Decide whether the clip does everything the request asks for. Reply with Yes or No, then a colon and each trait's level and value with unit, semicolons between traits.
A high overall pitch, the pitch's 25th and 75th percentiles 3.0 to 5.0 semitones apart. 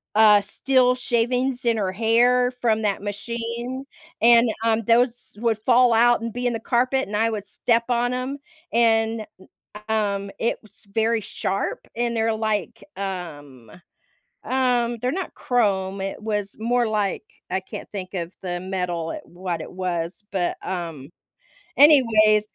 Yes: high, 225 Hz; average, 3.5 semitones